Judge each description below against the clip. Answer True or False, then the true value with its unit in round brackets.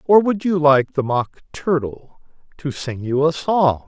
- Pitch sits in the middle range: True (150 Hz)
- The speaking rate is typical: True (185 wpm)